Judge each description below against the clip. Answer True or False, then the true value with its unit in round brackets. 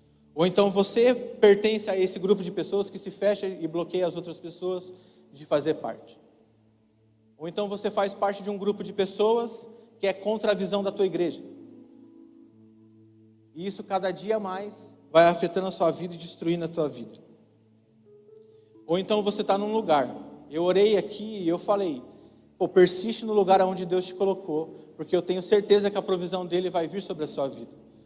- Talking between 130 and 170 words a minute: False (185 wpm)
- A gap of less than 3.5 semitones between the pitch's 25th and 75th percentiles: False (3.9 semitones)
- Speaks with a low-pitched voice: False (190 Hz)